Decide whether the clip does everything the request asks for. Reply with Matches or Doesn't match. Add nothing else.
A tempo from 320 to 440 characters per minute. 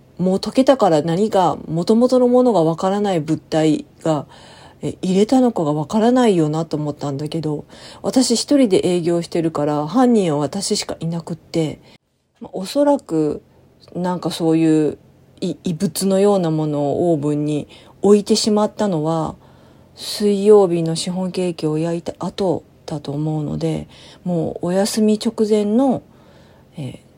Doesn't match